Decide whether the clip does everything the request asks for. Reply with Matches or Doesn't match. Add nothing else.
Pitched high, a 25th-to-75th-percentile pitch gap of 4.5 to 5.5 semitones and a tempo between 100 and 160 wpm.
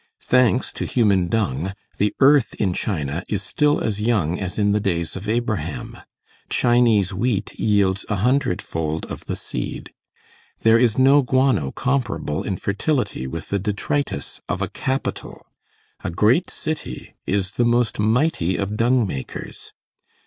Doesn't match